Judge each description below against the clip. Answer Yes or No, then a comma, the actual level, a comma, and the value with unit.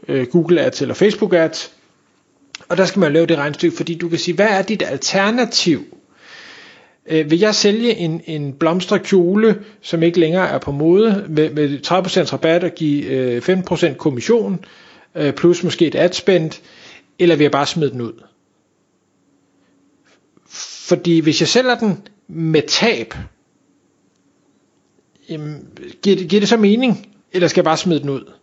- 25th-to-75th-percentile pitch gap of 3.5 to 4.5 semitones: Yes, average, 4.1 semitones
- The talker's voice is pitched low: No, medium, 175 Hz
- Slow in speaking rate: No, average, 160 wpm